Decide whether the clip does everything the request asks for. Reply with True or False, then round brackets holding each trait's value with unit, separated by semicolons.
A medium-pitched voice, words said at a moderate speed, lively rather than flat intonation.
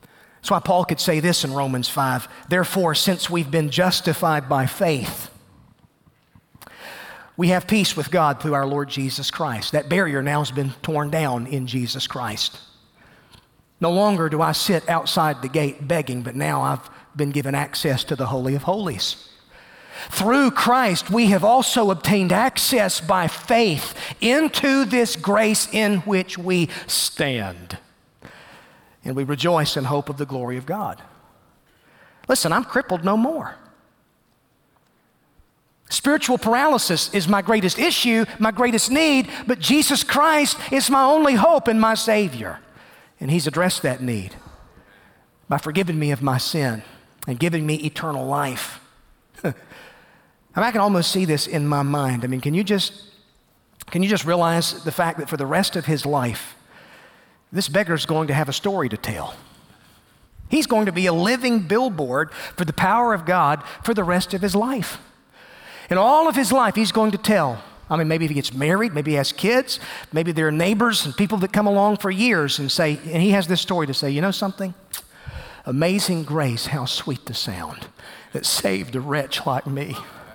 True (170 Hz; 175 wpm; 6.3 semitones)